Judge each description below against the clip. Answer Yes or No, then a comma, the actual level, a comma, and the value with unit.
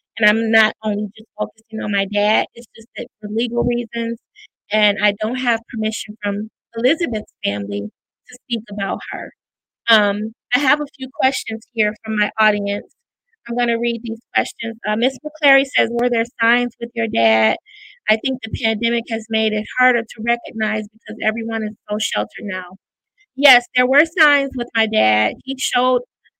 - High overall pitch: Yes, high, 225 Hz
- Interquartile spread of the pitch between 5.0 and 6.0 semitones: No, narrow, 2.5 semitones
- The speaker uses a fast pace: No, average, 175 wpm